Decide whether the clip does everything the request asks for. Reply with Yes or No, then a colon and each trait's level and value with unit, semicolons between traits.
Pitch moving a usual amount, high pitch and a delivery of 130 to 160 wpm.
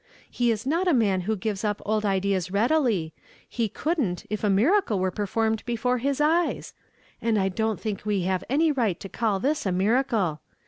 No: average, 4.5 semitones; high, 220 Hz; average, 190 wpm